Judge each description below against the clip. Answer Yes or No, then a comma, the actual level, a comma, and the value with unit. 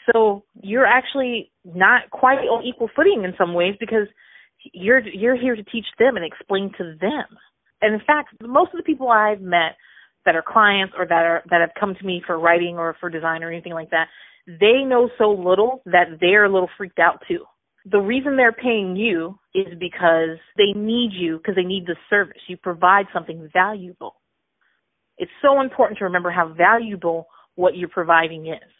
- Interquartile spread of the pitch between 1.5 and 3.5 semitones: No, average, 4.8 semitones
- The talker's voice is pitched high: Yes, high, 195 Hz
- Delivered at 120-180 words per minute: No, average, 190 wpm